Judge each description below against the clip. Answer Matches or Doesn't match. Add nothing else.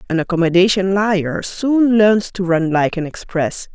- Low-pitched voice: Doesn't match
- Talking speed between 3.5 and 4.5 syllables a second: Matches